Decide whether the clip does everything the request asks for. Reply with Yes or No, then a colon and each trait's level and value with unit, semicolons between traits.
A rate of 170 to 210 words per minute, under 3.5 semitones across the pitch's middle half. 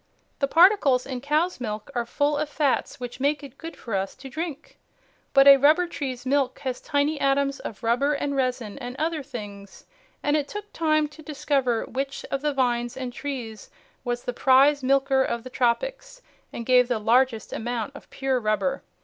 Yes: average, 185 wpm; average, 3.1 semitones